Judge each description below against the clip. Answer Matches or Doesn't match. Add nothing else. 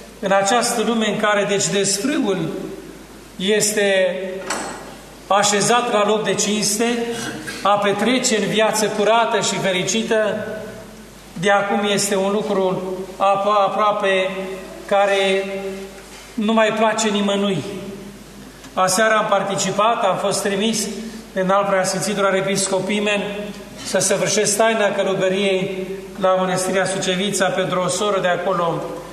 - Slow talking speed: Matches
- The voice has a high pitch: Matches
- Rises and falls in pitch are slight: Matches